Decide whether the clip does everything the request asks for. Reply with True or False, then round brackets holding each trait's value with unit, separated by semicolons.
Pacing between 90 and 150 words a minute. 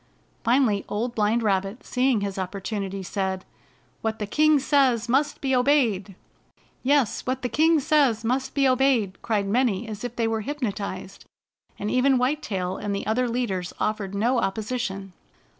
False (160 wpm)